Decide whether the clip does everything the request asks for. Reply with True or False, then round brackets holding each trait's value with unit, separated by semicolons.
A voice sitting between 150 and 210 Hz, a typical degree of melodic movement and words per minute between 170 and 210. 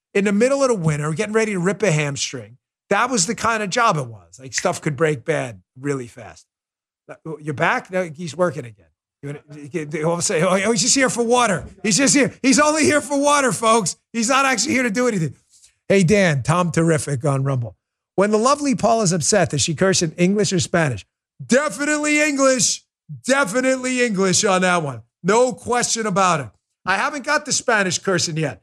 False (185 Hz; 8.2 semitones; 195 wpm)